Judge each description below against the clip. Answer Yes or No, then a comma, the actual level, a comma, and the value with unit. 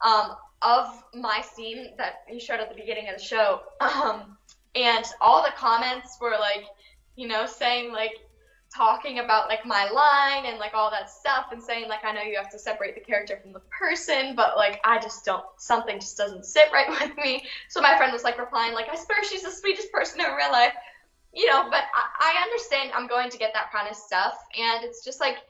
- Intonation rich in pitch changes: No, average, 3.7 semitones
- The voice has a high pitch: Yes, high, 230 Hz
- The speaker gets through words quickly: Yes, fast, 220 wpm